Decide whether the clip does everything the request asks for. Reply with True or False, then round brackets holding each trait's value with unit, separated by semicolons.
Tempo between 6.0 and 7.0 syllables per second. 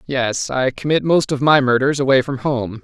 False (4.8 syllables/s)